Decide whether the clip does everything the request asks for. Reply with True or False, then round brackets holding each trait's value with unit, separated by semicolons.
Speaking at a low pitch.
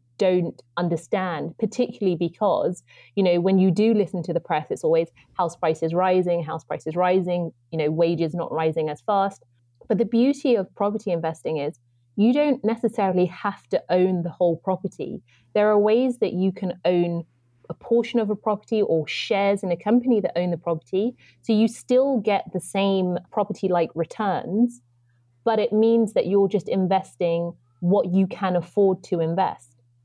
False (185 Hz)